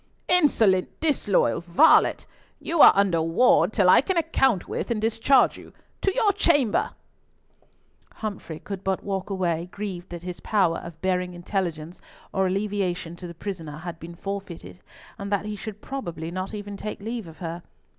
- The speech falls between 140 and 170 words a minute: Yes, average, 165 wpm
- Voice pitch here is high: Yes, high, 195 Hz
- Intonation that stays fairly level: No, average, 3.7 semitones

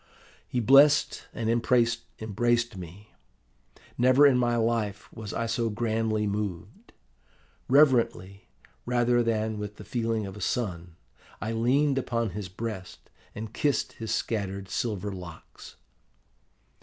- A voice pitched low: Yes, low, 115 Hz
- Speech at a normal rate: No, slow, 120 wpm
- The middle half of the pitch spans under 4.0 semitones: Yes, average, 2.7 semitones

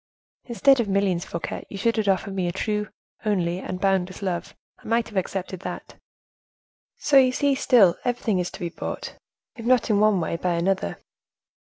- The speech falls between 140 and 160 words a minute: No, average, 185 wpm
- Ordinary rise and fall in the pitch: Yes, average, 4.1 semitones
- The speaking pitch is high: Yes, high, 195 Hz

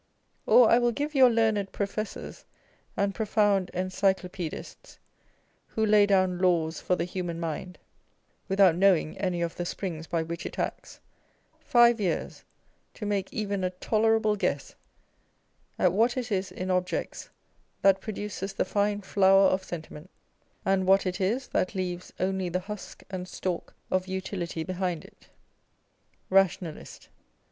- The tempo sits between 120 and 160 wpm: Yes, average, 140 wpm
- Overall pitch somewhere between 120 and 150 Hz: No, high, 190 Hz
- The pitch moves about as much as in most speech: No, narrow, 2.3 semitones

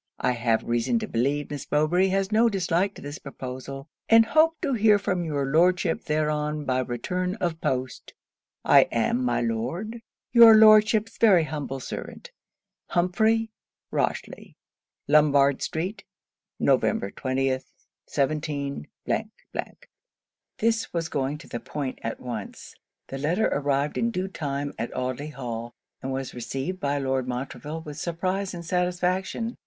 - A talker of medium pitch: Yes, medium, 150 Hz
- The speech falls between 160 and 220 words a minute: No, average, 140 wpm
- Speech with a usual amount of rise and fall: No, wide, 6.0 semitones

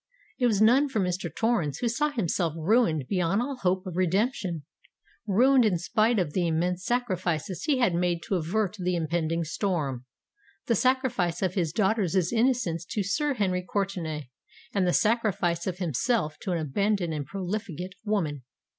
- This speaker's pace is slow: No, average, 155 wpm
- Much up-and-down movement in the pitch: No, average, 4.7 semitones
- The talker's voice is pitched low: No, medium, 185 Hz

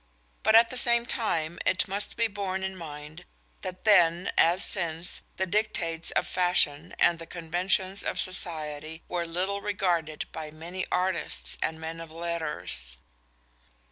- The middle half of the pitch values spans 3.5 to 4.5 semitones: No, average, 3.0 semitones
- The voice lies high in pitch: No, medium, 175 Hz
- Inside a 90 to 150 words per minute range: Yes, average, 145 wpm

